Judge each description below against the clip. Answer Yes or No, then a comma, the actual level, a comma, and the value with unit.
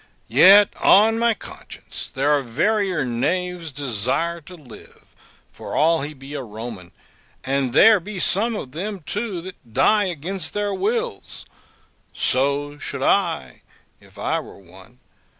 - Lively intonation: Yes, wide, 7.2 semitones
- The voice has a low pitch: No, medium, 160 Hz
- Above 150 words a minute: No, average, 140 wpm